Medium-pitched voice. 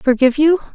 No: very high, 285 Hz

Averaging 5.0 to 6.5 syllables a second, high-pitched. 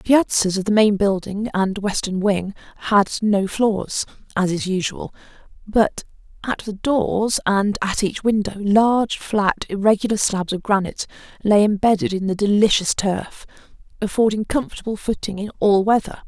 No: 4.7 syllables/s; high, 205 Hz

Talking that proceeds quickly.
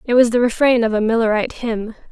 Yes: fast, 225 wpm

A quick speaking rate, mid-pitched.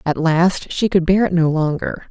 Yes: fast, 230 wpm; medium, 170 Hz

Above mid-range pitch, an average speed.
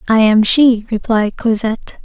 Yes: high, 225 Hz; average, 145 wpm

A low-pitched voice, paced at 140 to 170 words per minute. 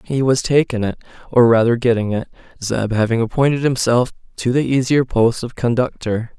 Yes: low, 120 Hz; average, 160 wpm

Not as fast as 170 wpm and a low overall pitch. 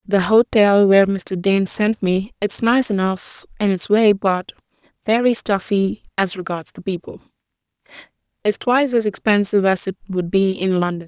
No: average, 150 wpm; high, 200 Hz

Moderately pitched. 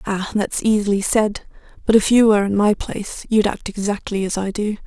No: high, 205 Hz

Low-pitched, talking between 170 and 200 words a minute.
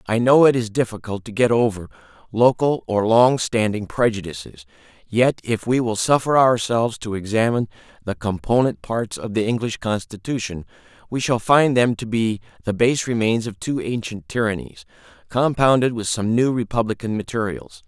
No: low, 110 Hz; average, 160 wpm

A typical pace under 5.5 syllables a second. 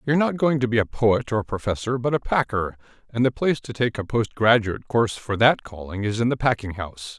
No: 6.1 syllables/s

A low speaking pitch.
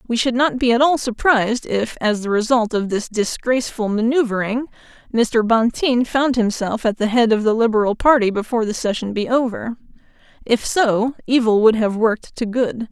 No: high, 230 Hz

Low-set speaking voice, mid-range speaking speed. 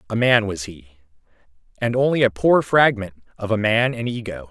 Yes: low, 110 Hz; average, 185 wpm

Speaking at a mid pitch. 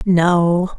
Yes: medium, 175 Hz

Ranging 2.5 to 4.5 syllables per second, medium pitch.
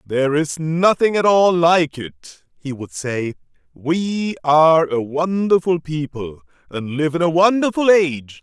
Yes: 4.1 syllables/s; medium, 160 Hz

